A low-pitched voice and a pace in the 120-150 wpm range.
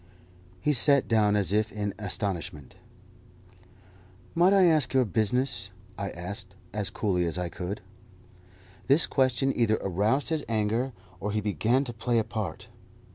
Yes: low, 110 Hz; average, 145 wpm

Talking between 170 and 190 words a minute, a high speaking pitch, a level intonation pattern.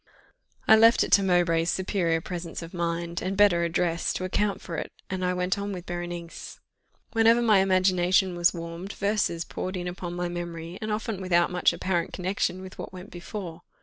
No: average, 185 wpm; medium, 180 Hz; narrow, 1.9 semitones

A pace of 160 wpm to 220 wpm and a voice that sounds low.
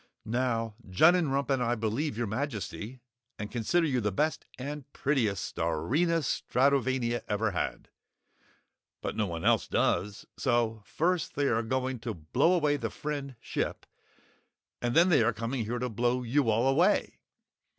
No: average, 150 wpm; low, 125 Hz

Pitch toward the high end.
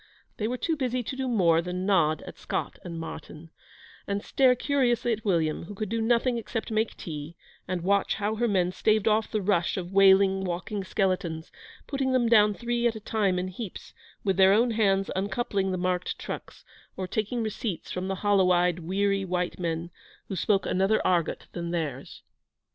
Yes: high, 195 Hz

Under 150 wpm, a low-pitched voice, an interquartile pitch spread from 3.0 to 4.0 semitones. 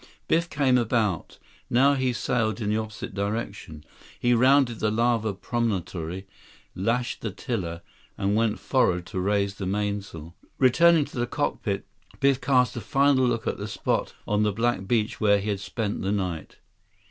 No: average, 165 wpm; low, 110 Hz; average, 3.7 semitones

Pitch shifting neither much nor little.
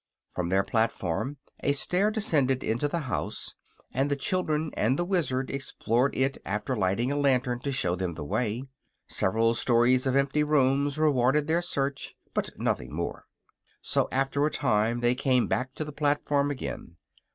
Yes: average, 3.4 semitones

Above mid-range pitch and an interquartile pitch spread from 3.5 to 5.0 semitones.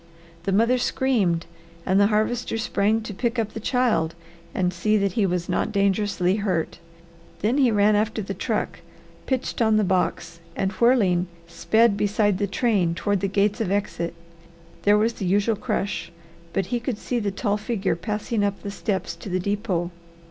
No: high, 205 Hz; average, 2.8 semitones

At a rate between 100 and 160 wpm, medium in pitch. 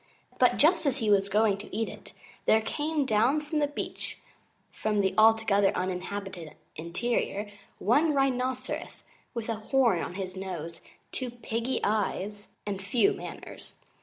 No: average, 145 wpm; high, 220 Hz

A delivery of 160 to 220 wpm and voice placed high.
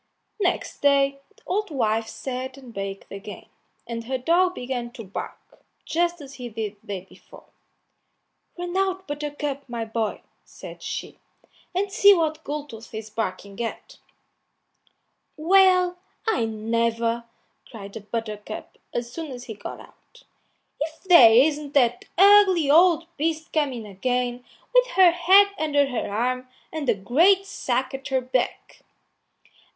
No: average, 140 wpm; very high, 265 Hz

